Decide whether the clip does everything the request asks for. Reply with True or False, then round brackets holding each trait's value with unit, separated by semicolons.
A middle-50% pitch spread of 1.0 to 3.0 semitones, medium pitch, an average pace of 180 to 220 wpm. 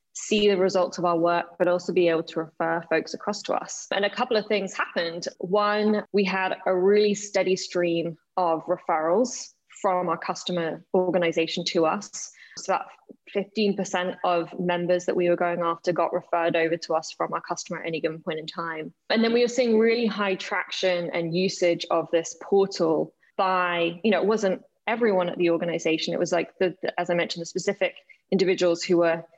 True (2.6 semitones; 180 Hz; 195 wpm)